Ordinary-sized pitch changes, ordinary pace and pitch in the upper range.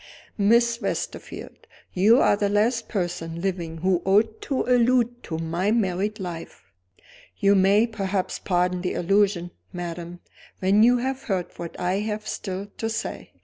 Yes: average, 3.9 semitones; average, 145 wpm; high, 195 Hz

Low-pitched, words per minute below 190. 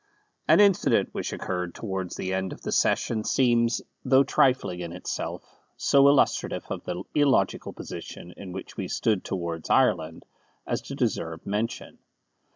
Yes: very low, 95 Hz; average, 150 wpm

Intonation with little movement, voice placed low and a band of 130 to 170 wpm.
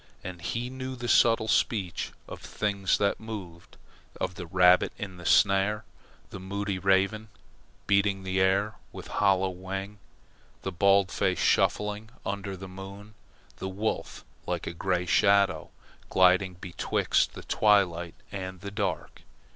Yes: narrow, 1.9 semitones; very low, 95 Hz; average, 140 wpm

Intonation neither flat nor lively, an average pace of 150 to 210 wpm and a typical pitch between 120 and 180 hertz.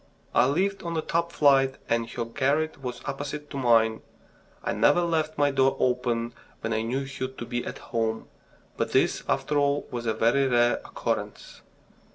Yes: average, 3.7 semitones; average, 180 wpm; low, 135 Hz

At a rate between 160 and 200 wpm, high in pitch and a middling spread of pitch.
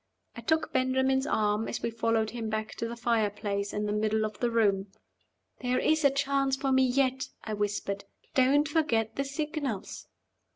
Yes: average, 180 wpm; high, 235 Hz; average, 3.9 semitones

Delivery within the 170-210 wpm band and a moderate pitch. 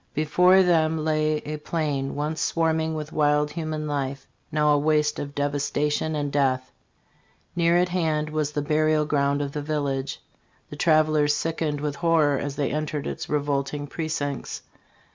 No: average, 155 wpm; medium, 150 Hz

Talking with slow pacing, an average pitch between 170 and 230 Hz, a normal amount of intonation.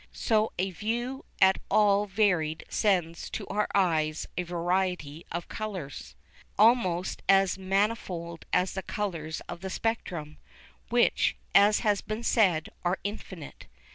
Yes: slow, 130 wpm; high, 190 Hz; average, 3.6 semitones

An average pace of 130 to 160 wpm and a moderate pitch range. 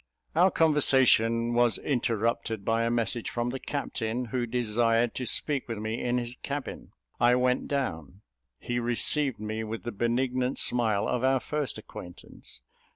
No: average, 155 wpm; narrow, 2.2 semitones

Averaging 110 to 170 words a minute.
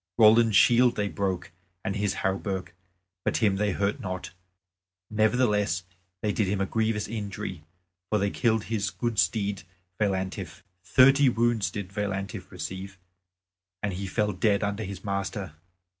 Yes: average, 145 wpm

